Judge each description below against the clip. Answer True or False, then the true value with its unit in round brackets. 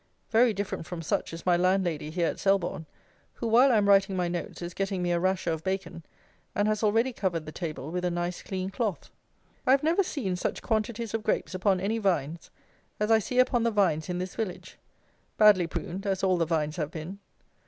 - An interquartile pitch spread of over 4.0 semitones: False (3.6 semitones)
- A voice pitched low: False (190 Hz)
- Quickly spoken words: True (215 wpm)